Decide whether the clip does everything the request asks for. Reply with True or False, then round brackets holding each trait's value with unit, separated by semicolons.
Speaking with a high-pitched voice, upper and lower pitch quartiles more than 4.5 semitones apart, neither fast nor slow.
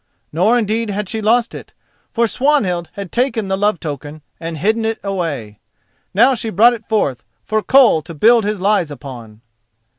True (205 Hz; 5.6 semitones; 175 wpm)